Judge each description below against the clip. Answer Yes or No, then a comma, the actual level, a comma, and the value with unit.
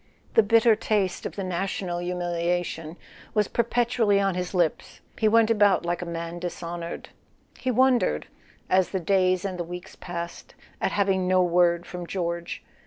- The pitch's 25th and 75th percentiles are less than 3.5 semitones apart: Yes, average, 2.7 semitones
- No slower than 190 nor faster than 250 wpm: No, average, 160 wpm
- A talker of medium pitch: Yes, medium, 180 Hz